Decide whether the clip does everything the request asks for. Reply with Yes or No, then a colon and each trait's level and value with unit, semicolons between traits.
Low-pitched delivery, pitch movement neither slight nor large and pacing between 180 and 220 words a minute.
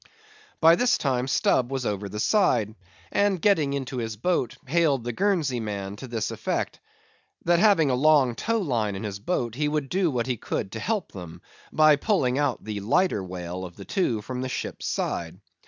No: low, 130 Hz; wide, 7.1 semitones; average, 190 wpm